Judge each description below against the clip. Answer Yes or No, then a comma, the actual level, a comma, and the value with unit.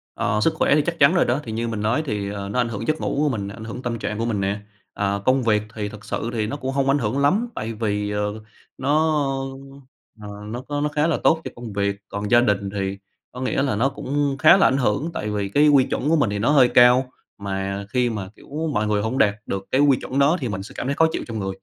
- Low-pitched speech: Yes, low, 115 Hz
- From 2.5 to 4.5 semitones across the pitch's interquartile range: No, average, 5.2 semitones